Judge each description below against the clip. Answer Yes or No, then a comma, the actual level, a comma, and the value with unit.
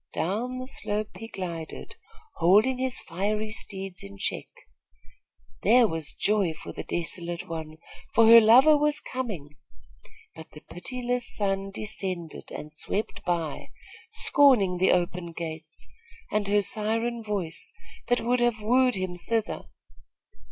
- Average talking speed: No, slow, 130 wpm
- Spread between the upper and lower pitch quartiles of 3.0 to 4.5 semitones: No, average, 5.2 semitones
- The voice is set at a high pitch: Yes, high, 200 Hz